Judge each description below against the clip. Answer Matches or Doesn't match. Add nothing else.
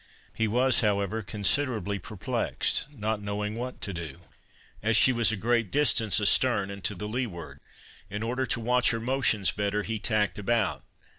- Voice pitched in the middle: Doesn't match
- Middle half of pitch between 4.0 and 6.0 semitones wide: Doesn't match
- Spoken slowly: Doesn't match